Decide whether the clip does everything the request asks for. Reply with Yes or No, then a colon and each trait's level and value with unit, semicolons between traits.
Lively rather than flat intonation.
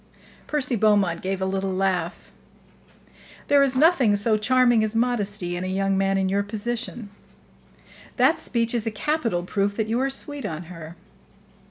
No: average, 4.0 semitones